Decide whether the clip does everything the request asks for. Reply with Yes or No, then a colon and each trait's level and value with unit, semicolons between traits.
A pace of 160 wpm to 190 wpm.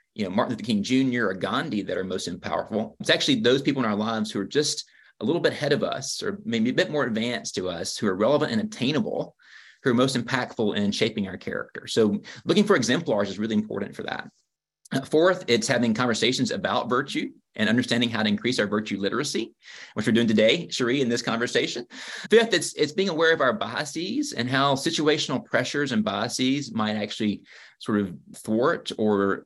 No: fast, 205 wpm